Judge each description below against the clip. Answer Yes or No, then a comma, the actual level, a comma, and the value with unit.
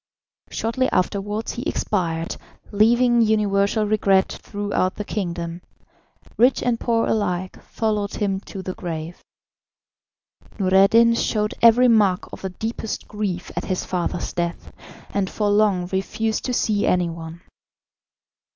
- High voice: Yes, high, 205 Hz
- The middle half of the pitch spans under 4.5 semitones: Yes, average, 3.3 semitones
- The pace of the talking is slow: Yes, slow, 125 wpm